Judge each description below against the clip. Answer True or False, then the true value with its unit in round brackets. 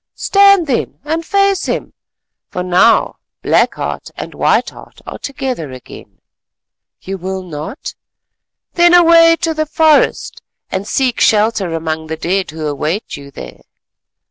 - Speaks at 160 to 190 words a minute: False (140 wpm)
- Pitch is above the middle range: True (215 Hz)